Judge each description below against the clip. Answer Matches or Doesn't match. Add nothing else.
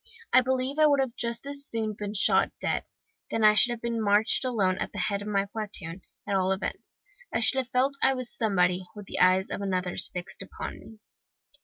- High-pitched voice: Matches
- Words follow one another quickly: Matches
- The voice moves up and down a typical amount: Matches